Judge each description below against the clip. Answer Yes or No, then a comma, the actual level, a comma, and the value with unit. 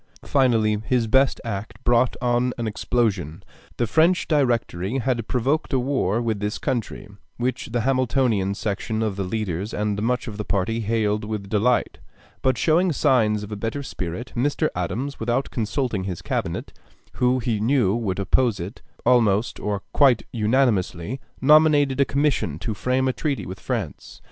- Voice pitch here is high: No, low, 115 Hz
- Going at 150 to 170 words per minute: Yes, average, 160 wpm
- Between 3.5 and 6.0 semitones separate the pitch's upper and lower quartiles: Yes, average, 3.9 semitones